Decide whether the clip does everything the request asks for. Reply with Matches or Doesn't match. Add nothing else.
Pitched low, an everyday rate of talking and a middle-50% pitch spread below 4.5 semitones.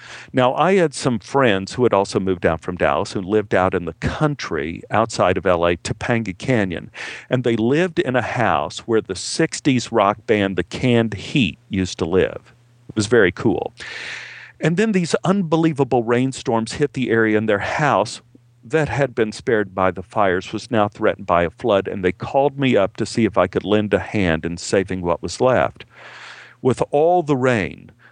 Doesn't match